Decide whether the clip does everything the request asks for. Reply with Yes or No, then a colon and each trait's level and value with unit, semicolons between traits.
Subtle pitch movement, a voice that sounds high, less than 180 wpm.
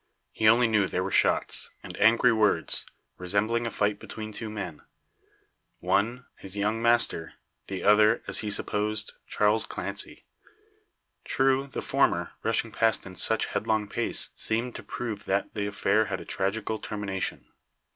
No: narrow, 2.0 semitones; low, 105 Hz; average, 150 wpm